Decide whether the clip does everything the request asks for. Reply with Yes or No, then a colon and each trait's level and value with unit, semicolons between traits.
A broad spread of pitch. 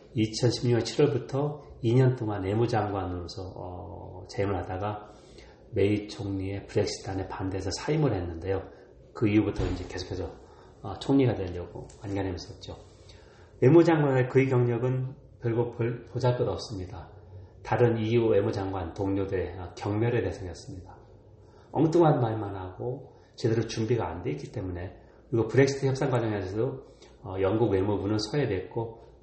No: average, 4.1 semitones